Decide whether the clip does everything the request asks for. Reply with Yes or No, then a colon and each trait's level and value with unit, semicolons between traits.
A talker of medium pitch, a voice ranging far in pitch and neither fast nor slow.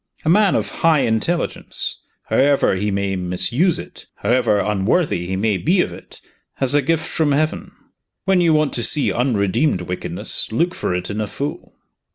No: low, 130 Hz; wide, 7.9 semitones; average, 175 wpm